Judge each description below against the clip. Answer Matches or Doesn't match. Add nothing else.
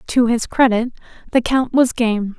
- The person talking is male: Doesn't match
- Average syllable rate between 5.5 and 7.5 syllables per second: Doesn't match